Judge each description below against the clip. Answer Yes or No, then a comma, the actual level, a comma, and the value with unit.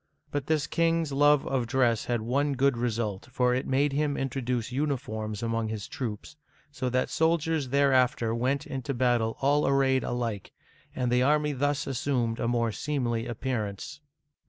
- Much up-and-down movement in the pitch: No, average, 3.2 semitones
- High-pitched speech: No, low, 130 Hz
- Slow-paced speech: No, average, 160 wpm